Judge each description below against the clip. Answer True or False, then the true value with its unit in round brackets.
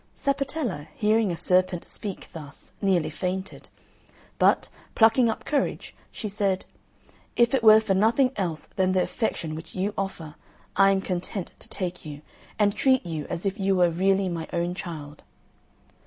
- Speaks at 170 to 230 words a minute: False (160 wpm)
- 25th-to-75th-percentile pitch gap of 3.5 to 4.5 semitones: True (3.8 semitones)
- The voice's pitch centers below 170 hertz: False (190 Hz)